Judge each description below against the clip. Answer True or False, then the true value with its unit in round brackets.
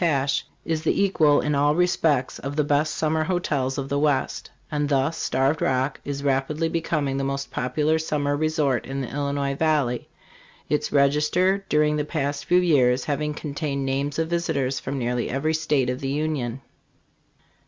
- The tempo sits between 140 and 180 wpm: True (170 wpm)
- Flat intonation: True (2.3 semitones)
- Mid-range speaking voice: True (145 Hz)